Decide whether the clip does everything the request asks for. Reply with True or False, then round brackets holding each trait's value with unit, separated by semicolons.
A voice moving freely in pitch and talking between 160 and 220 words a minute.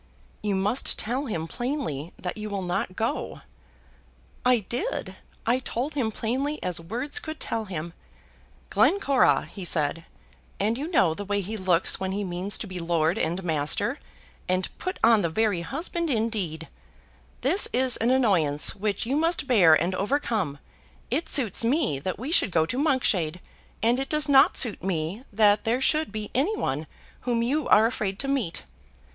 True (6.5 semitones; 170 wpm)